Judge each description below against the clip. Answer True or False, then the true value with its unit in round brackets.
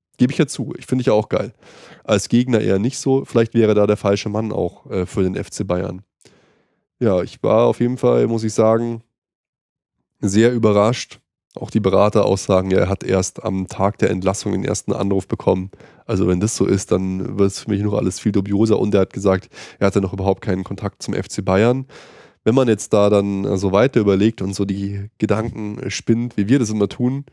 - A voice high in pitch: False (105 Hz)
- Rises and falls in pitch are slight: False (3.2 semitones)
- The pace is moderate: False (210 wpm)